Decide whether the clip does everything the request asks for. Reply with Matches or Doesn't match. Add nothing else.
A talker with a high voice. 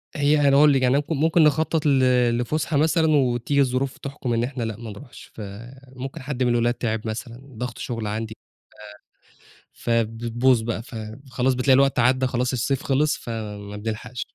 Doesn't match